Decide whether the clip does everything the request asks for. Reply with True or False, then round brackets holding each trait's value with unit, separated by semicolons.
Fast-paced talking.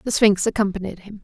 False (195 wpm)